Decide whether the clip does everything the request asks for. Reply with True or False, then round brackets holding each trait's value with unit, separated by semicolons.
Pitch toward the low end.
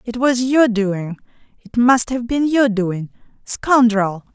False (230 Hz)